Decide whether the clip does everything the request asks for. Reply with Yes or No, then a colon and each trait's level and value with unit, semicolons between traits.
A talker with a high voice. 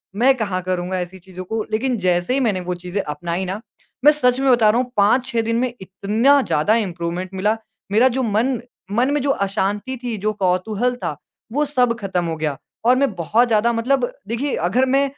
Yes: high, 220 Hz